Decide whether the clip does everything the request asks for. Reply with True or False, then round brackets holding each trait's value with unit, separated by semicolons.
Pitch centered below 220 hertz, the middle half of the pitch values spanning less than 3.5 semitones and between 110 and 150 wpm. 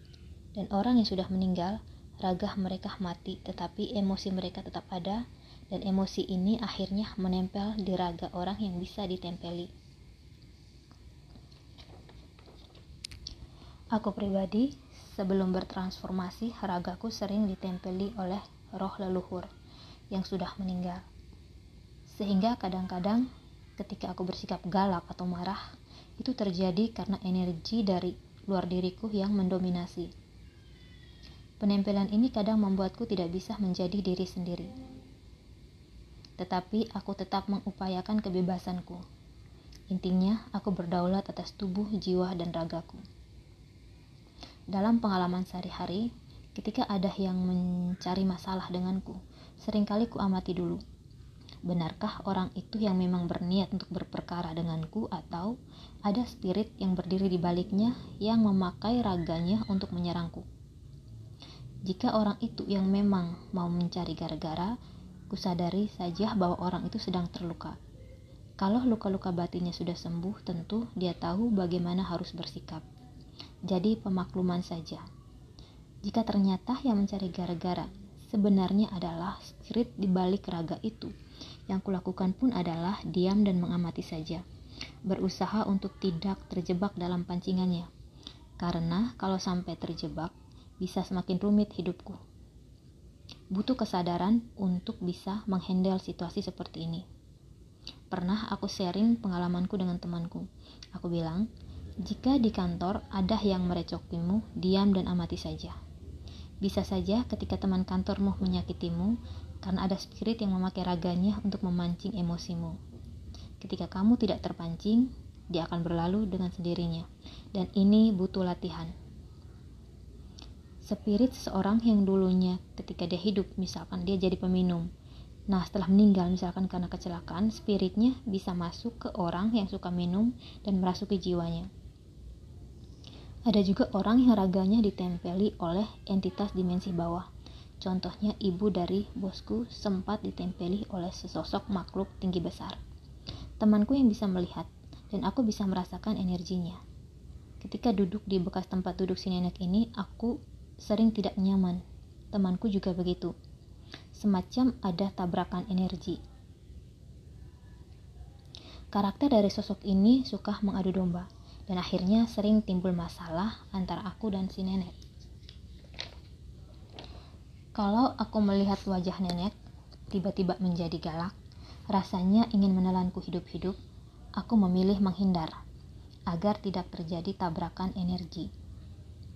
True (185 Hz; 2.4 semitones; 115 wpm)